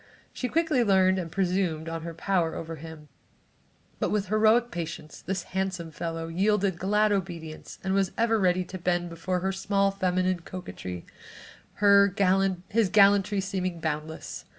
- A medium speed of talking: Yes, average, 145 wpm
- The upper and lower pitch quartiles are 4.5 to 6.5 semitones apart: No, average, 2.9 semitones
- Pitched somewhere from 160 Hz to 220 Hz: Yes, medium, 185 Hz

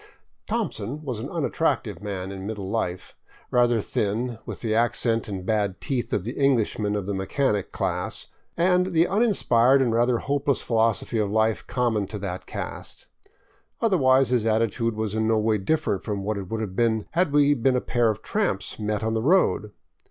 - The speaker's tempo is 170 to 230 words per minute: Yes, average, 185 wpm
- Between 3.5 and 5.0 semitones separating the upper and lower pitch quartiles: Yes, average, 3.9 semitones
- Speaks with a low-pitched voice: Yes, low, 115 Hz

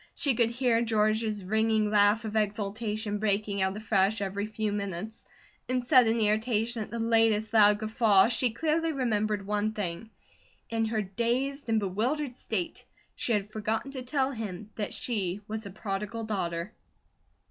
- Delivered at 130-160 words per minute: Yes, average, 150 wpm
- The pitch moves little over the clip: Yes, narrow, 2.0 semitones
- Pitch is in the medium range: No, high, 215 Hz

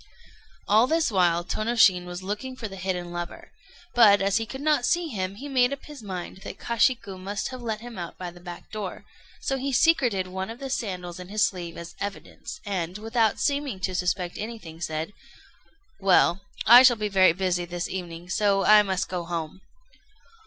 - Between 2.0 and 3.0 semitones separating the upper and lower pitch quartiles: No, average, 4.7 semitones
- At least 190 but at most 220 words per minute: Yes, average, 195 wpm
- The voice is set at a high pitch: Yes, high, 195 Hz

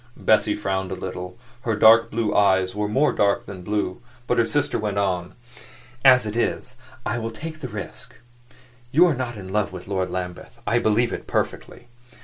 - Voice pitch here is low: Yes, low, 105 Hz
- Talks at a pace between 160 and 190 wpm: Yes, average, 185 wpm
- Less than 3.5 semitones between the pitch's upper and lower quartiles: No, average, 3.8 semitones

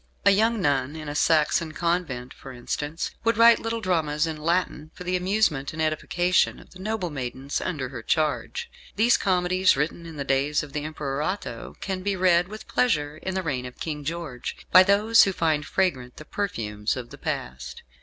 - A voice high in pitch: No, medium, 160 Hz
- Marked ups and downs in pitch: No, average, 4.7 semitones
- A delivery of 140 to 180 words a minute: No, average, 195 wpm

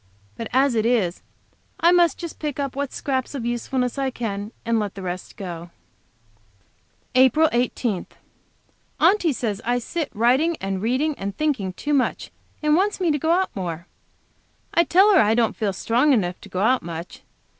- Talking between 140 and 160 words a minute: No, average, 175 wpm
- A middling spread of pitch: No, wide, 6.5 semitones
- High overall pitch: Yes, high, 245 Hz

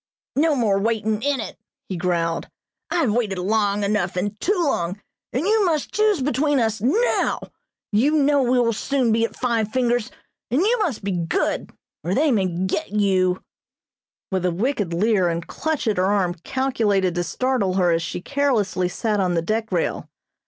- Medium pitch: No, high, 220 Hz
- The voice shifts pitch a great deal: Yes, wide, 6.3 semitones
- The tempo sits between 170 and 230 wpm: Yes, average, 180 wpm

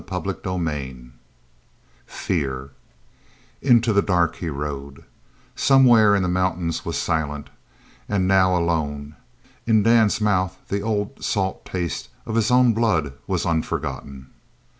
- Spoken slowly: Yes, slow, 120 wpm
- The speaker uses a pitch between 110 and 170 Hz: No, very low, 90 Hz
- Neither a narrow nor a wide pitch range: No, wide, 6.0 semitones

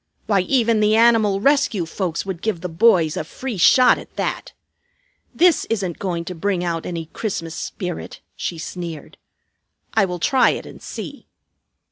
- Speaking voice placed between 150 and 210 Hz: Yes, high, 190 Hz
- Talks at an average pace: Yes, average, 160 wpm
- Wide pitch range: No, average, 4.8 semitones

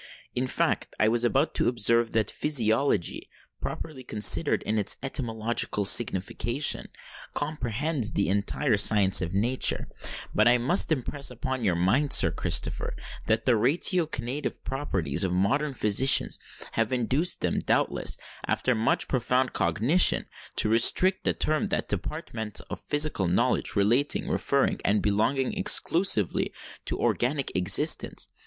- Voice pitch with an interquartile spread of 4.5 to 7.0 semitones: Yes, average, 5.0 semitones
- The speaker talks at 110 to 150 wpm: Yes, slow, 135 wpm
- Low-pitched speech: Yes, low, 120 Hz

